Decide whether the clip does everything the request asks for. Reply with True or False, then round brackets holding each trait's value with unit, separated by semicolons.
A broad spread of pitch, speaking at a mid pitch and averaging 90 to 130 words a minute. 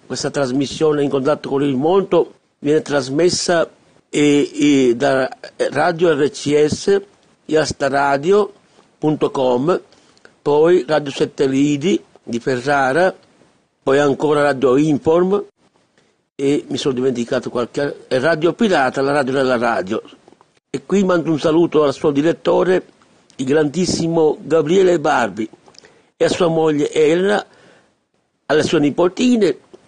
False (3.3 semitones; 145 Hz; 115 wpm)